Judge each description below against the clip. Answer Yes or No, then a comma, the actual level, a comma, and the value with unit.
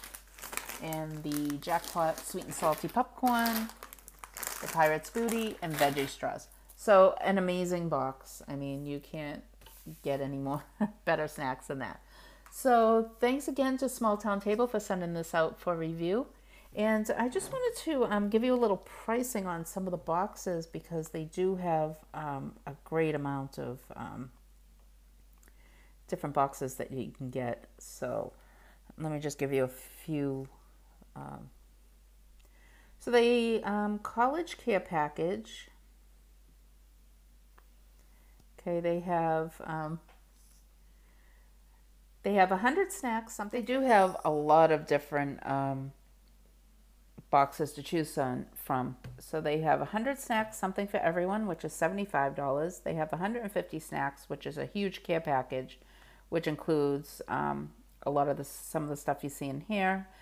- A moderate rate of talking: Yes, average, 145 wpm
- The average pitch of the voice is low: No, medium, 160 Hz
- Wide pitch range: Yes, wide, 6.5 semitones